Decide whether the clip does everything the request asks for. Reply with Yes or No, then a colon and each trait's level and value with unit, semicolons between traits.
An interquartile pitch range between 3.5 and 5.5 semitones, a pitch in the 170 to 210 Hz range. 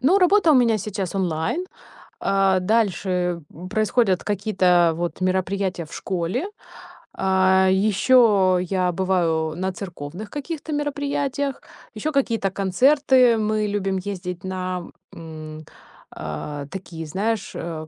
Yes: average, 4.2 semitones; high, 190 Hz